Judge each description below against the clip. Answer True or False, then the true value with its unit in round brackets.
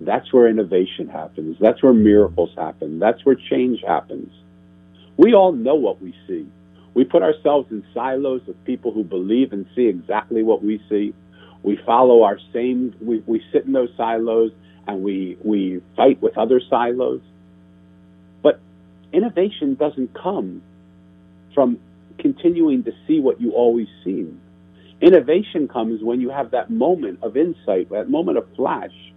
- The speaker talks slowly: False (155 wpm)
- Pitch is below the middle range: True (110 Hz)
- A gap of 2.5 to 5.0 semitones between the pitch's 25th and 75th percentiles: False (5.4 semitones)